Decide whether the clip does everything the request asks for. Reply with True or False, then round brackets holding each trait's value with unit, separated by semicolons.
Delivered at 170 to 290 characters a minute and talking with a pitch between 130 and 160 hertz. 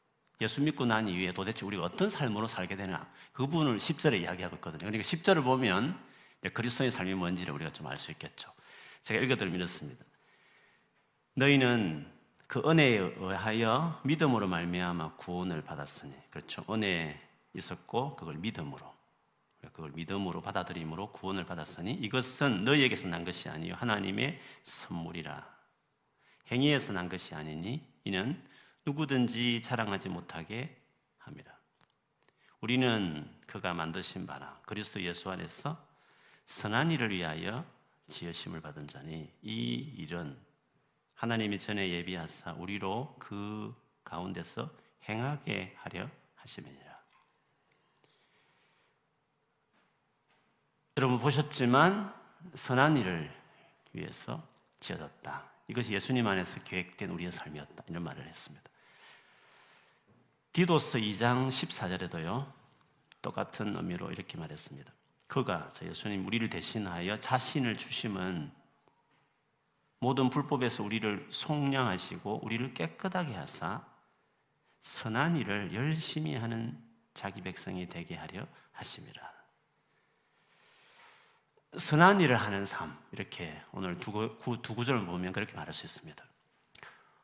False (280 characters per minute; 110 Hz)